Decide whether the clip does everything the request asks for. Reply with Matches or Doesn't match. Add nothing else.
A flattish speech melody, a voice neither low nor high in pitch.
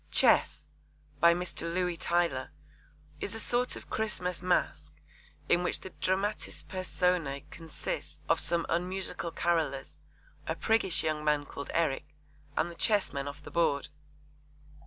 Doesn't match